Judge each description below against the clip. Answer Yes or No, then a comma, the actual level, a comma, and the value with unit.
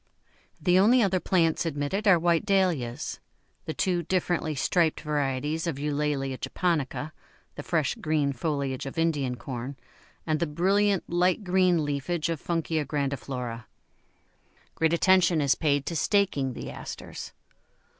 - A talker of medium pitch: Yes, medium, 160 Hz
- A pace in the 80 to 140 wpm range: Yes, slow, 135 wpm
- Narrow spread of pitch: No, average, 3.9 semitones